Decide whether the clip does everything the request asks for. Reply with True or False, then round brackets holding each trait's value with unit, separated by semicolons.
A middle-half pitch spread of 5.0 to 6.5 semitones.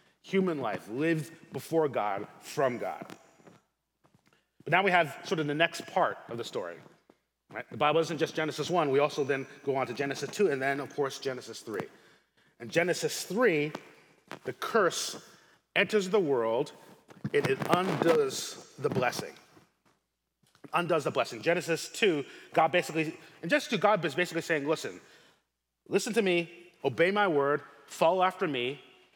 False (3.9 semitones)